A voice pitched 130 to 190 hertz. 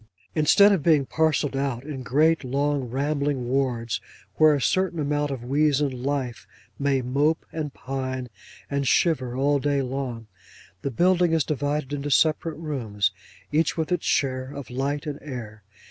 Yes: medium, 140 Hz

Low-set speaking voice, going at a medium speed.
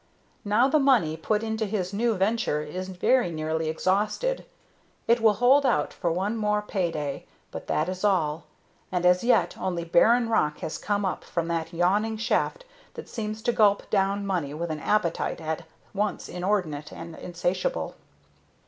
No: high, 190 Hz; average, 165 wpm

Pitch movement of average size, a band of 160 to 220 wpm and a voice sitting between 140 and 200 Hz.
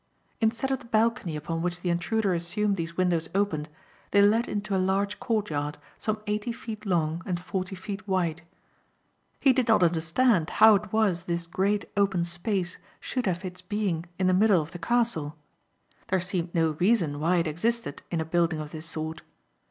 Yes: average, 3.9 semitones; average, 185 wpm; medium, 185 Hz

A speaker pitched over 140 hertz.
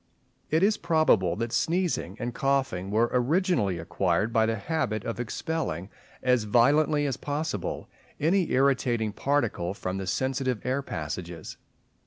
No: low, 120 Hz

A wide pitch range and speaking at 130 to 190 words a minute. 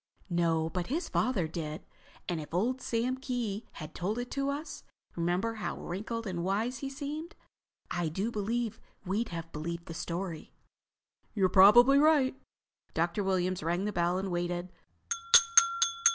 Yes: wide, 5.7 semitones; average, 140 wpm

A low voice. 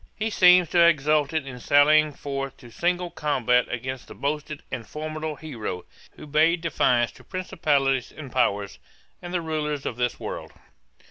No: medium, 150 Hz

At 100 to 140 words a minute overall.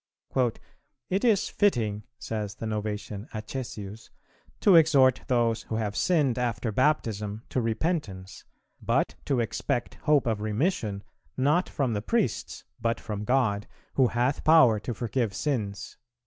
Yes: slow, 135 wpm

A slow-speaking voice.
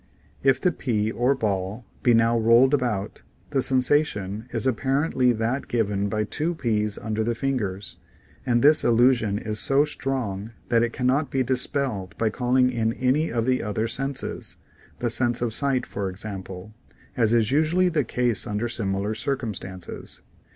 No: average, 160 wpm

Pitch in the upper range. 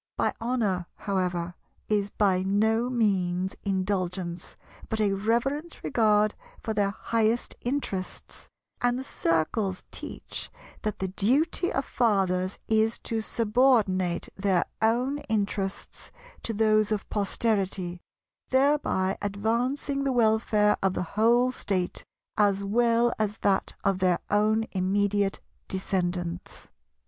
Yes: high, 210 Hz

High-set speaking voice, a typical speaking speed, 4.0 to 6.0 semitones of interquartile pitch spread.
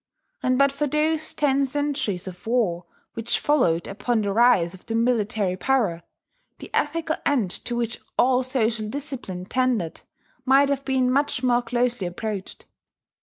Yes: high, 245 Hz; average, 150 wpm; average, 4.7 semitones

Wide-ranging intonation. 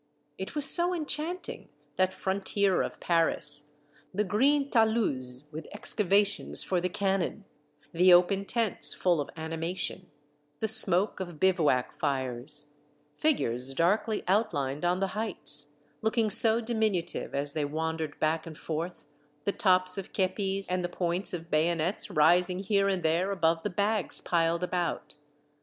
No: average, 4.2 semitones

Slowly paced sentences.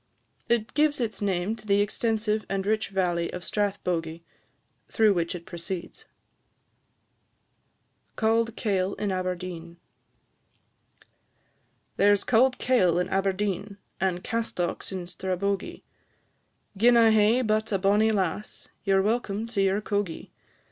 Yes: slow, 125 wpm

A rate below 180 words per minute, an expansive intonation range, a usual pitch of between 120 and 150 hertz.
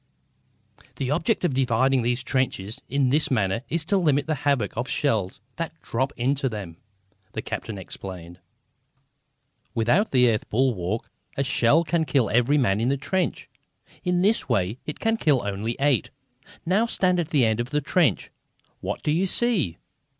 Yes: average, 165 wpm; wide, 5.7 semitones; low, 135 Hz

